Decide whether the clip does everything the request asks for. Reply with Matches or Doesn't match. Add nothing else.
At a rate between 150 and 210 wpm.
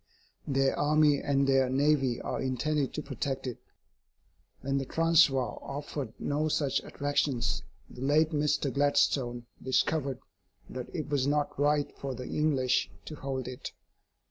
Doesn't match